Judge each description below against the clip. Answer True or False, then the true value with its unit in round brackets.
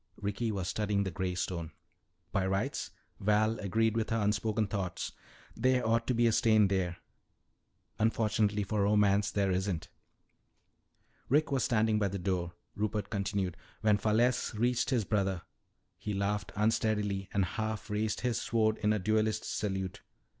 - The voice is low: True (105 Hz)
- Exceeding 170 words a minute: False (150 wpm)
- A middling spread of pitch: False (2.1 semitones)